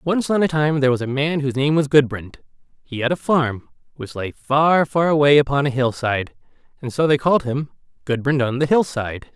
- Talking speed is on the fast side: Yes, fast, 225 wpm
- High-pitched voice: No, medium, 140 Hz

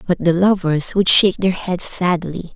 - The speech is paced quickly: No, average, 190 wpm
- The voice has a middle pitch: Yes, medium, 180 Hz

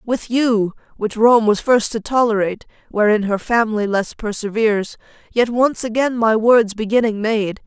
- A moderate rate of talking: Yes, average, 155 wpm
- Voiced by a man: No, female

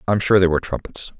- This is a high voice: No, very low, 90 Hz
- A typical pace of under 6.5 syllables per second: No, 6.9 syllables/s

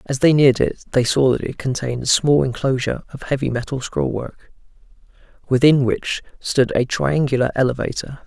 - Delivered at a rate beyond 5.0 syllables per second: Yes, 5.4 syllables/s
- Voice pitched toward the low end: Yes, low, 130 Hz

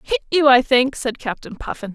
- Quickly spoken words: Yes, fast, 215 wpm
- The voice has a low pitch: No, very high, 265 Hz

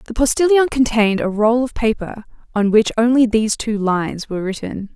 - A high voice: Yes, high, 225 Hz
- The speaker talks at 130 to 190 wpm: Yes, average, 180 wpm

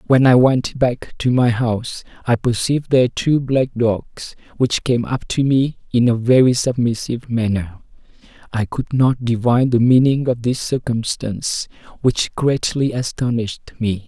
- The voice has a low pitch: Yes, low, 120 Hz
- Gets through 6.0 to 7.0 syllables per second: No, 4.6 syllables/s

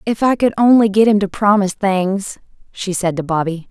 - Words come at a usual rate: No, fast, 210 wpm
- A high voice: Yes, high, 200 Hz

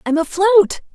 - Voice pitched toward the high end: Yes, very high, 375 Hz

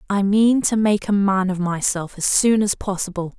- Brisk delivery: Yes, fast, 215 wpm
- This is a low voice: No, high, 195 Hz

